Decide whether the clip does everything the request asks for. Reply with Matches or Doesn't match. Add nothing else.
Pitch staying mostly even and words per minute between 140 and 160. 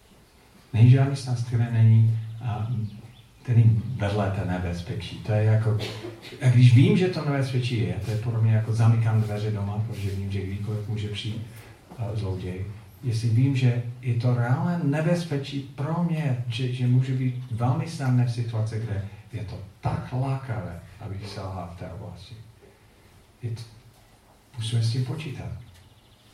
Doesn't match